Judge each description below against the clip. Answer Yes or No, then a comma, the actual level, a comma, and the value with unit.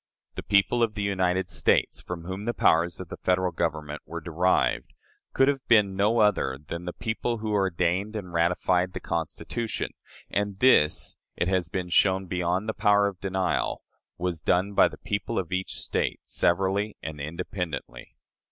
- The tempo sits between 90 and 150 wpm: No, average, 170 wpm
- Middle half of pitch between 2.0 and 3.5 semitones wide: Yes, average, 3.0 semitones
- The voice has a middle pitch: No, very low, 95 Hz